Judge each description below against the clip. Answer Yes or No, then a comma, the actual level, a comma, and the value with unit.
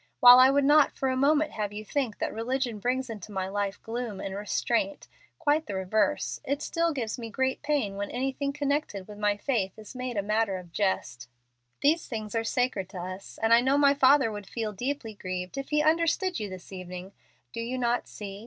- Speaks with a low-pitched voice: No, high, 230 Hz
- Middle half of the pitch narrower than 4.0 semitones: No, average, 5.2 semitones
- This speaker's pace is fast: Yes, fast, 210 wpm